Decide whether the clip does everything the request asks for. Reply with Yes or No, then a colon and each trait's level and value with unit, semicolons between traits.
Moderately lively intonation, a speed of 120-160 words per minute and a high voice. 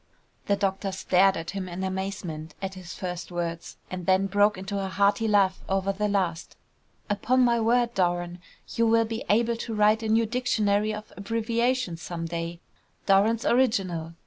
No: average, 3.5 semitones; average, 170 wpm; high, 195 Hz